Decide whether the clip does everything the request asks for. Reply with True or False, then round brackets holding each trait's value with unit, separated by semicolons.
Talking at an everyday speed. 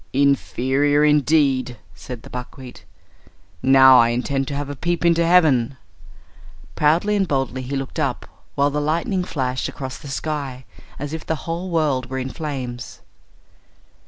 True (150 wpm)